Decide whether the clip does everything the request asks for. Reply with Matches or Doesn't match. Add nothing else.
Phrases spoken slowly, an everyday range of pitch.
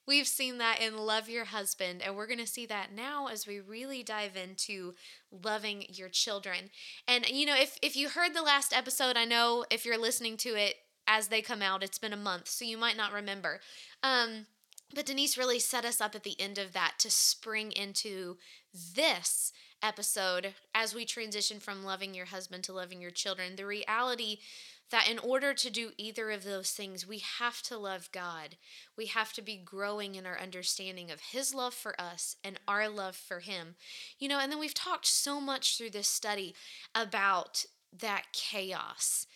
Doesn't match